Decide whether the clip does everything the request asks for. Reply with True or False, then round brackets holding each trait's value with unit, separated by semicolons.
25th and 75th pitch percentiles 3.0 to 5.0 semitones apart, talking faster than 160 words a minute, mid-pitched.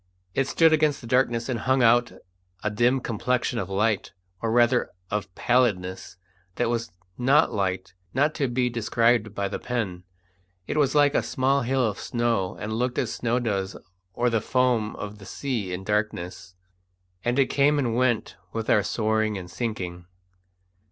False (3.5 semitones; 170 wpm; 115 Hz)